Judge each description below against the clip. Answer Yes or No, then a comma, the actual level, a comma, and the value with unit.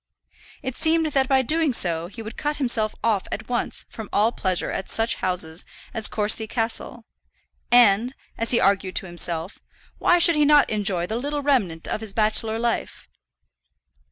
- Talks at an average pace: Yes, average, 170 wpm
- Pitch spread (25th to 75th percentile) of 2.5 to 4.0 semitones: No, average, 5.0 semitones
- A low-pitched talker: No, high, 225 Hz